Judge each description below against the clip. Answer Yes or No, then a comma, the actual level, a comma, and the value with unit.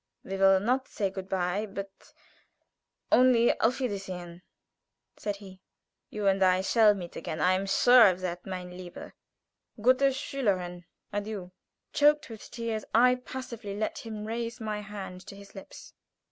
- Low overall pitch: No, high, 200 Hz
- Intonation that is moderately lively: Yes, average, 3.6 semitones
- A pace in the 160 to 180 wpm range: No, average, 150 wpm